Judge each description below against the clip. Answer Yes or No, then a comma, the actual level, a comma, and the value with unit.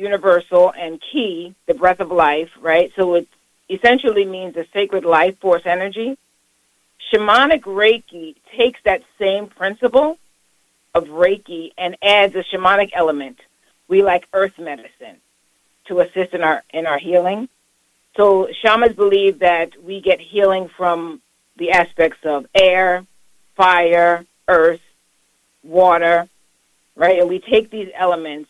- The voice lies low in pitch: No, medium, 180 Hz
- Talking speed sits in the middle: No, slow, 130 wpm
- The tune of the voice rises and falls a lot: No, average, 2.7 semitones